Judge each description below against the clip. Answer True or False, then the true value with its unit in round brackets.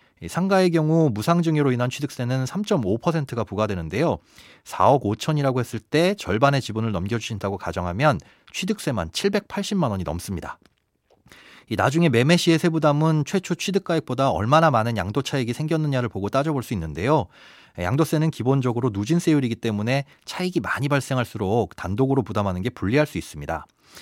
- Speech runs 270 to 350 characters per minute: False (365 characters per minute)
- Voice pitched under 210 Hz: True (135 Hz)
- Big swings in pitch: True (6.7 semitones)